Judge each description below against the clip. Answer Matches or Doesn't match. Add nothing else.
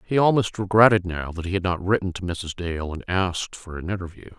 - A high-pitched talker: Doesn't match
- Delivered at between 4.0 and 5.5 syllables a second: Doesn't match